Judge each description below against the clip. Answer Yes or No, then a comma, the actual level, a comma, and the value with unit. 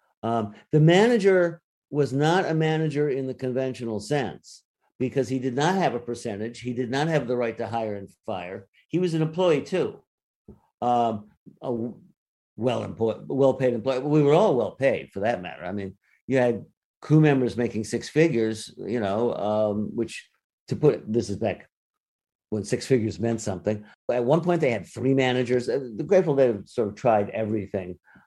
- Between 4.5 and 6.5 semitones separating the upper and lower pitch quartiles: Yes, average, 4.9 semitones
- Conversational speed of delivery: Yes, average, 185 wpm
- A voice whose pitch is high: No, low, 125 Hz